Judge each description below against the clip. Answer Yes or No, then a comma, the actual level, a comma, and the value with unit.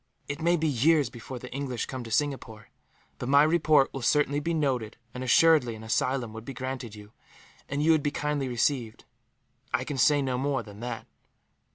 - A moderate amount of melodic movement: Yes, average, 3.6 semitones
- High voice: No, low, 135 Hz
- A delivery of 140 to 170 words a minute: No, average, 195 wpm